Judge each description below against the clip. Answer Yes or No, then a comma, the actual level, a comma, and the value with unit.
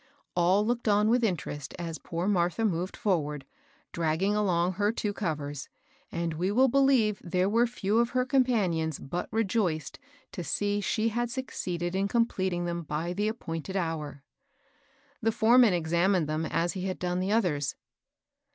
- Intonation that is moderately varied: Yes, average, 4.4 semitones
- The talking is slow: No, average, 165 wpm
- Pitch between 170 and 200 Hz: Yes, medium, 185 Hz